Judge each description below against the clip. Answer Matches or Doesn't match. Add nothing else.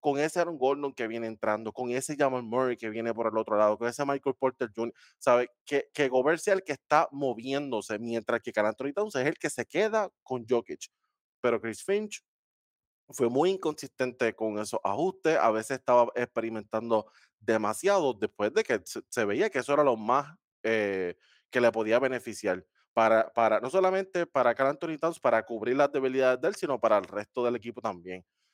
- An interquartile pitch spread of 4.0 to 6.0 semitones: Matches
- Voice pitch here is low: Matches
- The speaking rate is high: Matches